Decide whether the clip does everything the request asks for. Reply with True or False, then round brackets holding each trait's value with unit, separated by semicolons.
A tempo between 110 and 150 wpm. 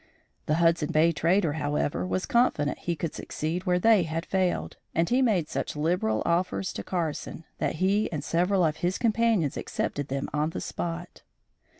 False (175 wpm)